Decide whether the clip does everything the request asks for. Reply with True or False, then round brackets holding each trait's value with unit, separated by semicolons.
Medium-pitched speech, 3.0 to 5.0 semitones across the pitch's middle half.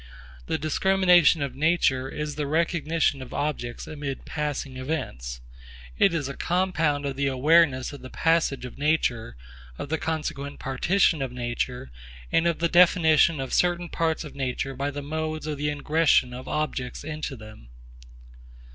True (150 Hz; 3.4 semitones)